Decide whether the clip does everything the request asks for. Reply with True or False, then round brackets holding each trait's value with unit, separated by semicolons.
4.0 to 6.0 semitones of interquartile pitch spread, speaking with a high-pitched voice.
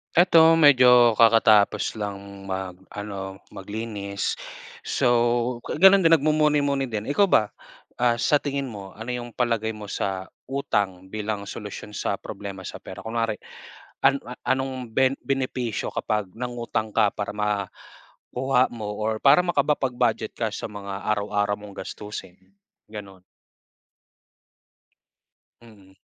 False (4.3 semitones; 110 Hz)